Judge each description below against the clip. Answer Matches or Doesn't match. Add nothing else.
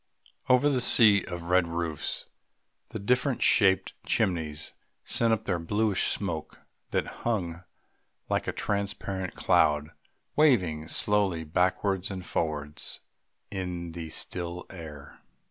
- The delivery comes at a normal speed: Doesn't match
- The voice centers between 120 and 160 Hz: Doesn't match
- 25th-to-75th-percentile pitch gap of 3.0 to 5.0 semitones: Matches